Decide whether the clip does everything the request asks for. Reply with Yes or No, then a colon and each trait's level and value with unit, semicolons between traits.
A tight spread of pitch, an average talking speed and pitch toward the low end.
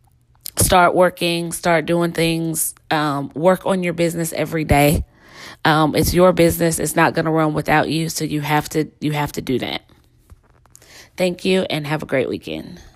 No: narrow, 2.1 semitones; average, 180 wpm; medium, 160 Hz